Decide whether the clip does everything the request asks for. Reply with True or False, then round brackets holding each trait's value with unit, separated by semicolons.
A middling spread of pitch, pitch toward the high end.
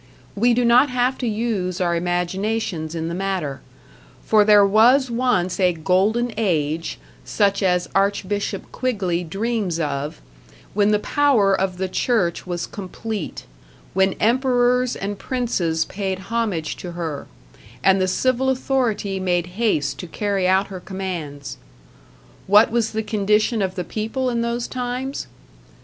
True (4.6 semitones; 200 Hz)